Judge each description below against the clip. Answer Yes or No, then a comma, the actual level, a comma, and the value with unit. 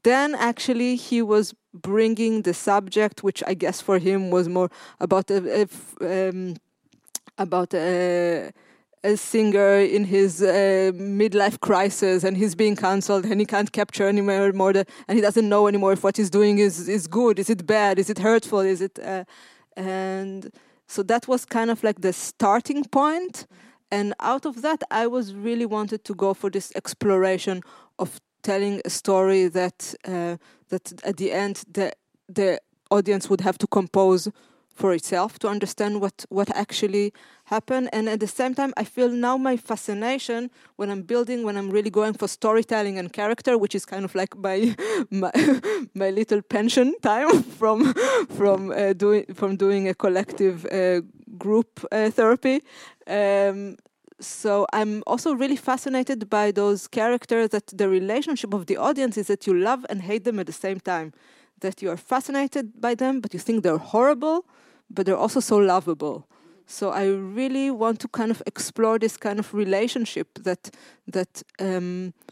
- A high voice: Yes, high, 205 Hz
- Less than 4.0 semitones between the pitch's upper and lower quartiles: Yes, average, 3.4 semitones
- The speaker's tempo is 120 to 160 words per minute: No, average, 170 wpm